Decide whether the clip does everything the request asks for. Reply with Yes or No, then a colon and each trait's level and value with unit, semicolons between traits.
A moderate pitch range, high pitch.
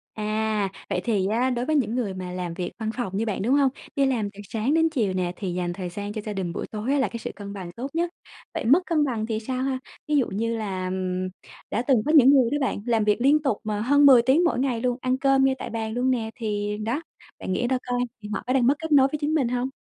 Yes: average, 4.4 semitones; high, 230 Hz